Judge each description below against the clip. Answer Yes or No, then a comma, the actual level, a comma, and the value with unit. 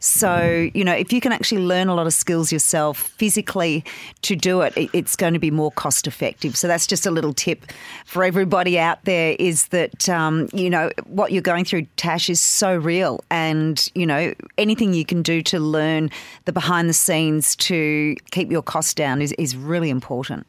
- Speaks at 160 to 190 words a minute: No, average, 200 wpm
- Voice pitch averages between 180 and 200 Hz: No, medium, 170 Hz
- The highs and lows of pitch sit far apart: No, narrow, 2.6 semitones